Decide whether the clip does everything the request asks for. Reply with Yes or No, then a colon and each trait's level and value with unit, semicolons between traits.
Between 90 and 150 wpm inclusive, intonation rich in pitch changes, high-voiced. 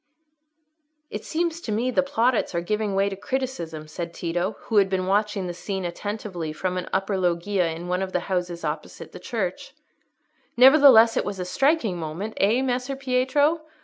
No: average, 180 wpm; wide, 6.0 semitones; high, 200 Hz